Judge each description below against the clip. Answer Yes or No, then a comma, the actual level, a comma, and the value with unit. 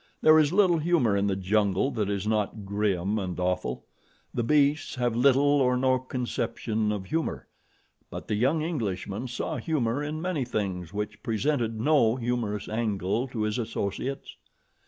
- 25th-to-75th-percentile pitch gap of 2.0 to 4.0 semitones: No, average, 5.2 semitones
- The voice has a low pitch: Yes, low, 115 Hz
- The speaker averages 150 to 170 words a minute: Yes, average, 155 wpm